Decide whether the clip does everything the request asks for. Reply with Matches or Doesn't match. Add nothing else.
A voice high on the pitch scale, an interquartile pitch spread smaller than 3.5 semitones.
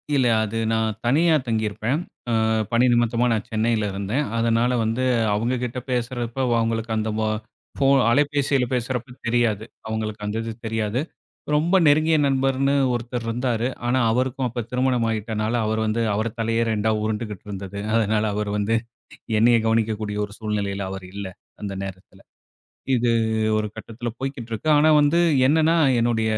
Doesn't match